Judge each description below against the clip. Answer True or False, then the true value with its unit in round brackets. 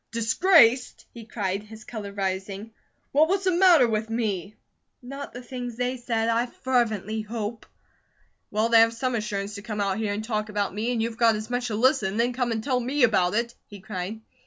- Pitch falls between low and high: False (225 Hz)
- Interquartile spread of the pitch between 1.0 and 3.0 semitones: True (2.7 semitones)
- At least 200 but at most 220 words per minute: True (205 wpm)